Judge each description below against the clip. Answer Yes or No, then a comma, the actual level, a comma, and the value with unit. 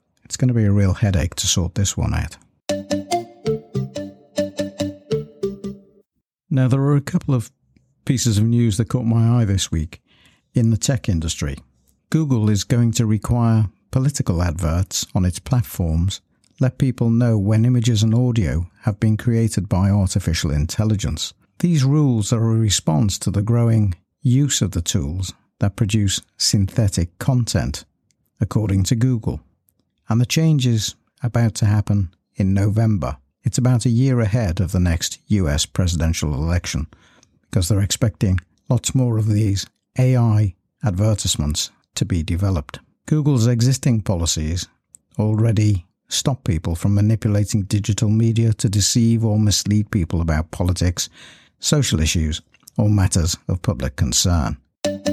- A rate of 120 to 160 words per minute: Yes, average, 140 wpm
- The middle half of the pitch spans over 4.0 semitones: Yes, average, 4.5 semitones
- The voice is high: No, low, 105 Hz